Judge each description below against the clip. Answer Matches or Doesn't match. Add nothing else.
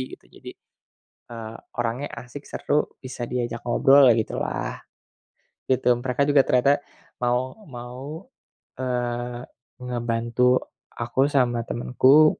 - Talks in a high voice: Doesn't match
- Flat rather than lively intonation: Matches